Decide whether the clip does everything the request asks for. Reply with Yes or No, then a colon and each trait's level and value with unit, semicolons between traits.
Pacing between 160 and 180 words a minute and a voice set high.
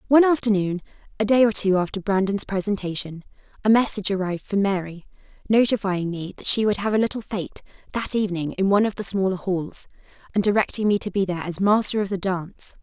No: average, 195 wpm; high, 195 Hz